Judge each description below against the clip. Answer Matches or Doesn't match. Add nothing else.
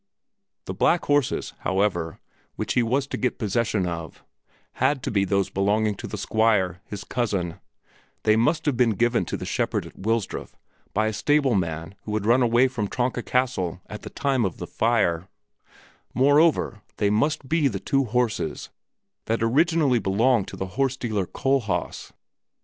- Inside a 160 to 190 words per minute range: Matches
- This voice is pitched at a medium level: Doesn't match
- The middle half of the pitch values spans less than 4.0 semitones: Doesn't match